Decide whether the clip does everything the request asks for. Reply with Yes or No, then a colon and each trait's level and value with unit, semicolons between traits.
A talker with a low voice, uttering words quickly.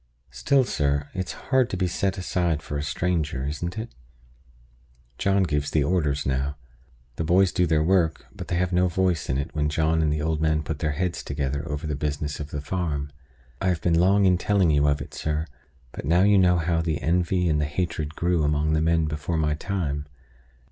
Yes: very low, 80 Hz; fast, 210 wpm